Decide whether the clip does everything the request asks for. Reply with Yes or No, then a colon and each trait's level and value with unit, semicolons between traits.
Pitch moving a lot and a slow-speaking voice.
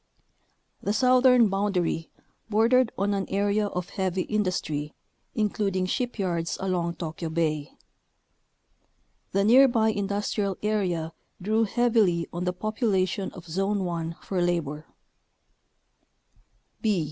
No: average, 3.6 semitones; slow, 105 wpm